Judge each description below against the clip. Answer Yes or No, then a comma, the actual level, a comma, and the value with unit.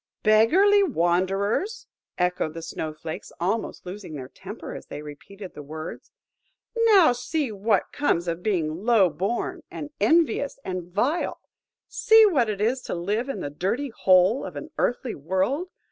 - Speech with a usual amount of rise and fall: No, wide, 8.0 semitones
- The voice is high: Yes, high, 205 Hz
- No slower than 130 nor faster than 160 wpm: Yes, average, 155 wpm